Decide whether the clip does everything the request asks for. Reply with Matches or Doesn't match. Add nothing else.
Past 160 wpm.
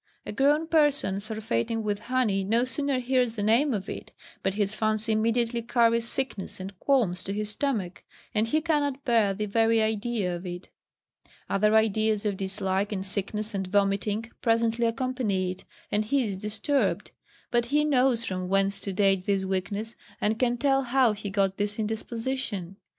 Matches